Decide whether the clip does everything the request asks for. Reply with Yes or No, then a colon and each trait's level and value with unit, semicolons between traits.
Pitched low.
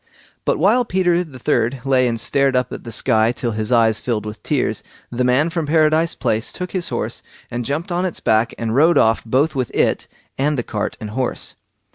Yes: low, 130 Hz